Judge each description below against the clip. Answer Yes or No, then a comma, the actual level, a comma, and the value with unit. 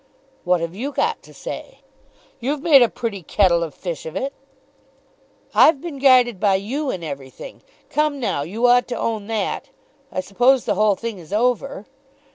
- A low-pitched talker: No, high, 230 Hz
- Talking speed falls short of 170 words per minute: No, average, 175 wpm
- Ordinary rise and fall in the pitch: No, wide, 6.3 semitones